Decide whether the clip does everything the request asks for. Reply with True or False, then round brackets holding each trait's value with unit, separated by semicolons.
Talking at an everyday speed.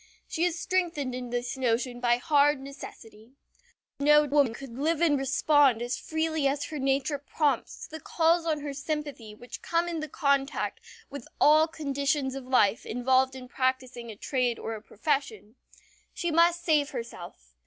True (165 wpm)